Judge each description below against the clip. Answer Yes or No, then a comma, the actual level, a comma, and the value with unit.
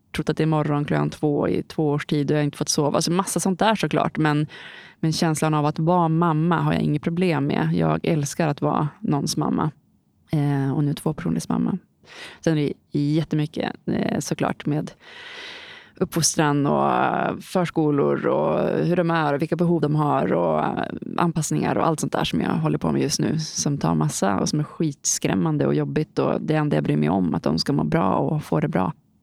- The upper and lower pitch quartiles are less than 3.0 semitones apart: Yes, narrow, 2.4 semitones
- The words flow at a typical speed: No, fast, 215 wpm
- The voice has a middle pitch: Yes, medium, 155 Hz